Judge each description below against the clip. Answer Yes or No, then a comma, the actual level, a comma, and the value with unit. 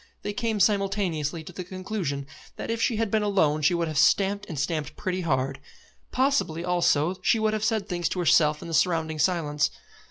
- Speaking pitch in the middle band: Yes, medium, 180 Hz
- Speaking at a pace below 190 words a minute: No, average, 195 wpm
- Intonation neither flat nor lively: Yes, average, 4.9 semitones